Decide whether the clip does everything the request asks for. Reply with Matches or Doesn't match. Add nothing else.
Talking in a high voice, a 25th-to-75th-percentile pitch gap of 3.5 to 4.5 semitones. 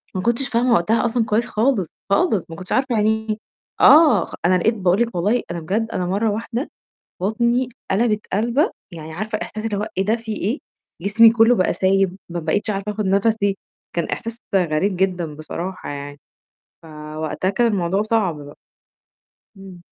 Matches